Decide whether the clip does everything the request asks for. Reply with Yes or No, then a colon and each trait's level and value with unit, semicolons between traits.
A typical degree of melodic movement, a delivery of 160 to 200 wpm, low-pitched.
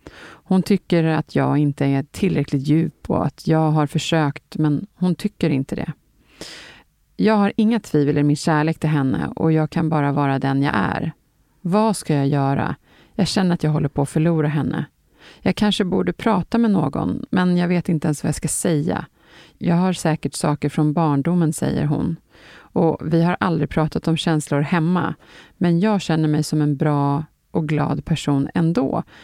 No: average, 3.0 semitones; average, 185 wpm; medium, 160 Hz